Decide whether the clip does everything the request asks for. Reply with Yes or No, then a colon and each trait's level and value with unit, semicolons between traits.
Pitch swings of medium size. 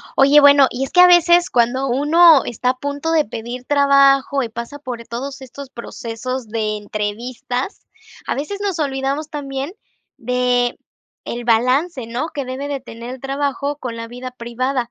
Yes: average, 3.0 semitones